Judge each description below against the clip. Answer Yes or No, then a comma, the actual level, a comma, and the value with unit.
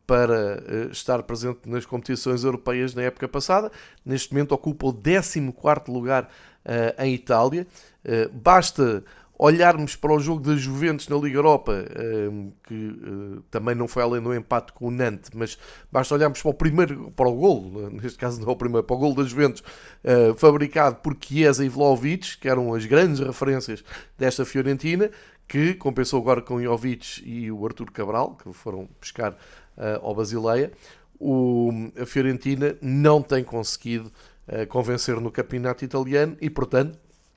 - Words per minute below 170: Yes, average, 155 wpm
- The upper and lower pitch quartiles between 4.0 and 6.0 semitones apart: No, average, 3.6 semitones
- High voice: No, low, 130 Hz